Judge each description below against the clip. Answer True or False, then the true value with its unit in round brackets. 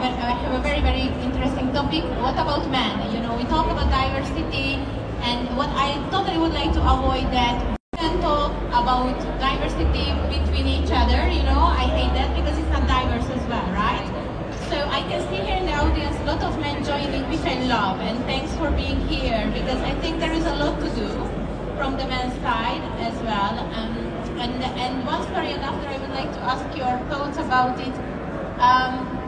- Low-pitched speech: False (240 Hz)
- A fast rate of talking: False (195 wpm)